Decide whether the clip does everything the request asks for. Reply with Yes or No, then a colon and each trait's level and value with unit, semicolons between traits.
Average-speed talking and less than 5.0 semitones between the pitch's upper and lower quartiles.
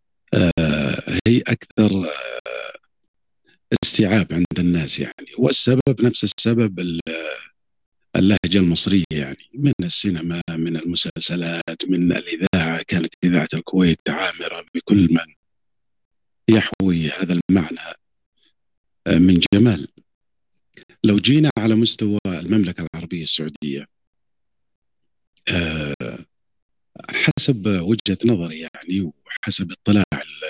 Yes: average, 85 wpm; average, 4.2 semitones